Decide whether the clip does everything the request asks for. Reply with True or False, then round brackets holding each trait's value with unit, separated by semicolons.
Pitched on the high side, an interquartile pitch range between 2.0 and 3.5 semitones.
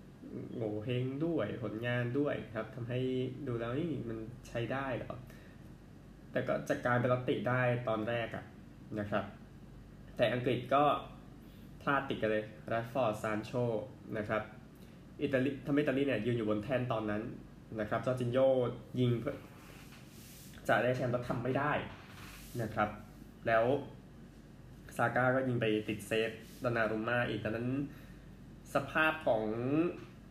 False (120 Hz; 3.2 semitones)